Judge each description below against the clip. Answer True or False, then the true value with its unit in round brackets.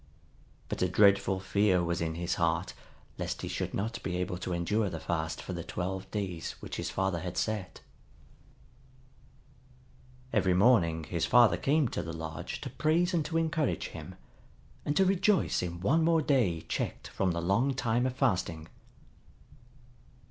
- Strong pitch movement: True (6.6 semitones)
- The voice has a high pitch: False (95 Hz)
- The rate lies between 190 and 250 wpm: False (165 wpm)